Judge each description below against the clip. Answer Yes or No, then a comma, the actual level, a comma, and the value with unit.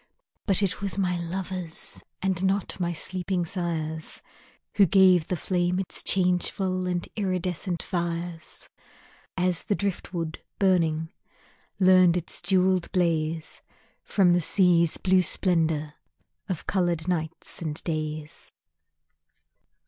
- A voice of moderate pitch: Yes, medium, 180 Hz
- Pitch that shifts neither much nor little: No, narrow, 2.1 semitones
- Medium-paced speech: No, slow, 110 wpm